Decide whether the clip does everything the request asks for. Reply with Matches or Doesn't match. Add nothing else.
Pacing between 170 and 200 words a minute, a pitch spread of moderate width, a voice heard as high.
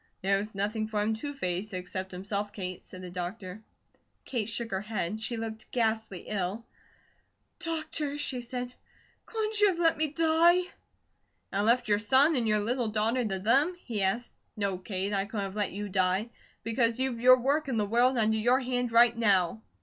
Matches